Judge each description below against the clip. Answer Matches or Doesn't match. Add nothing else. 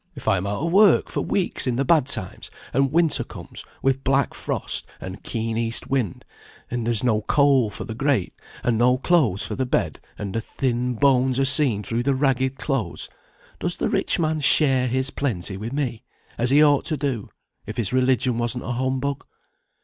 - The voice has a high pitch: Doesn't match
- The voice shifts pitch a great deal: Doesn't match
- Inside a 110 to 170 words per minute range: Doesn't match